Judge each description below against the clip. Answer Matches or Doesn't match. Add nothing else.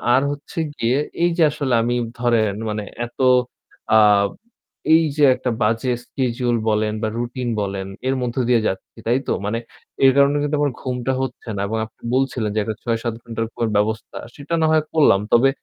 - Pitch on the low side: Matches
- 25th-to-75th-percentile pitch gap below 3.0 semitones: Doesn't match